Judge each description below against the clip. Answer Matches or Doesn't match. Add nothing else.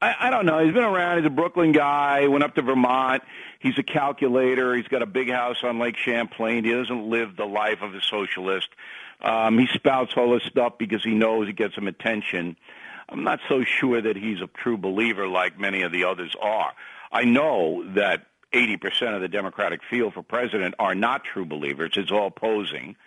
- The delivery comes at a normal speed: Doesn't match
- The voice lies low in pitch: Matches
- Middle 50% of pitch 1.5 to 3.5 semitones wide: Doesn't match